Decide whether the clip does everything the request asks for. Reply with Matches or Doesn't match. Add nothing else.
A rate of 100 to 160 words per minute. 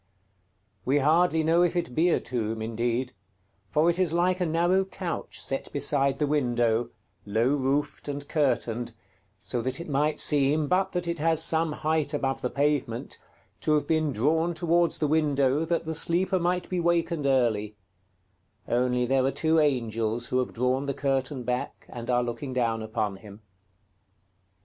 Doesn't match